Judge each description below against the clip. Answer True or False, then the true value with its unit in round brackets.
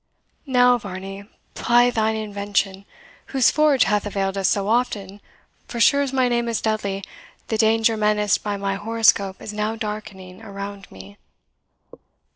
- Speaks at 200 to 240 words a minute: False (145 wpm)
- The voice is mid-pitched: False (210 Hz)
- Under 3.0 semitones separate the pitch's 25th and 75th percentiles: True (2.6 semitones)